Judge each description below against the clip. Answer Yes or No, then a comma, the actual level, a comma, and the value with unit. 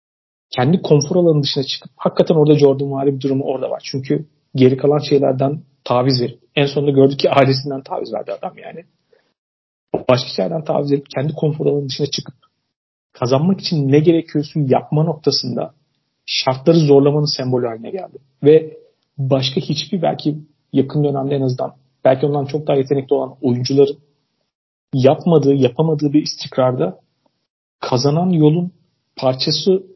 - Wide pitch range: No, narrow, 2.6 semitones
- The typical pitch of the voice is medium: Yes, medium, 145 Hz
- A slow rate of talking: No, fast, 140 wpm